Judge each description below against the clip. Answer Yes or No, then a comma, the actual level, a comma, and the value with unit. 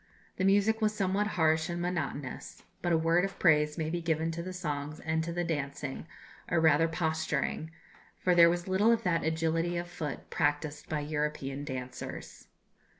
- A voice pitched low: No, medium, 165 Hz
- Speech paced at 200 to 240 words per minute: No, average, 175 wpm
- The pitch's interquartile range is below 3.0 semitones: Yes, narrow, 2.6 semitones